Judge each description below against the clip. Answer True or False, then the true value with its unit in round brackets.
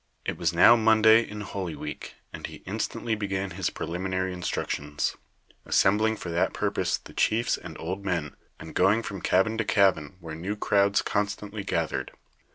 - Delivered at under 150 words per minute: False (165 wpm)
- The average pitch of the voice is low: True (95 Hz)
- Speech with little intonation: False (3.6 semitones)